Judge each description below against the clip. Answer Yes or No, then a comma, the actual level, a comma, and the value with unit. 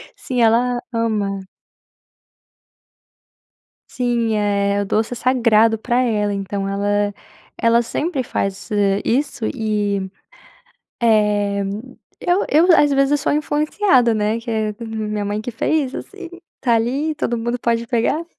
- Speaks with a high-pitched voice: Yes, high, 230 Hz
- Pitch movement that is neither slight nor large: Yes, average, 3.5 semitones